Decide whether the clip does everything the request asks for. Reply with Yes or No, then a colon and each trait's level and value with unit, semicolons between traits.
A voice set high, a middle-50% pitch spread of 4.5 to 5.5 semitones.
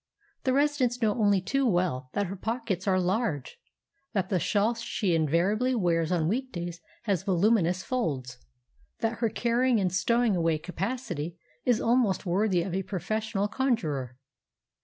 Yes: high, 195 Hz; average, 5.1 semitones